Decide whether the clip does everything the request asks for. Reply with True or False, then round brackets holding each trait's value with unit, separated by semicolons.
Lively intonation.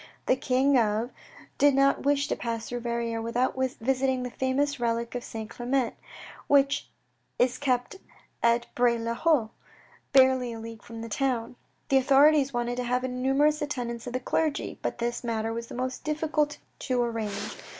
False (2.6 semitones)